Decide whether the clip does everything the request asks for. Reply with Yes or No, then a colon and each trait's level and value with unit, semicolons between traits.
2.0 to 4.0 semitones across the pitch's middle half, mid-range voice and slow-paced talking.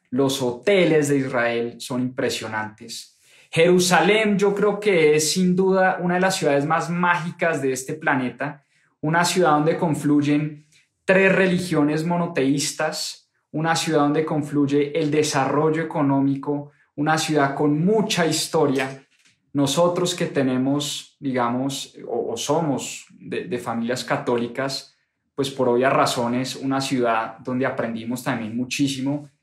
Yes: average, 3.6 semitones; medium, 145 Hz; slow, 125 wpm